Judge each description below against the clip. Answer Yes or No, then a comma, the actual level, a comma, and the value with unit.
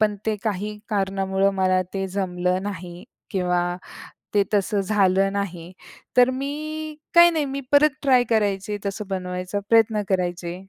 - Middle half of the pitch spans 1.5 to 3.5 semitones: Yes, average, 3.2 semitones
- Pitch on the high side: Yes, high, 200 Hz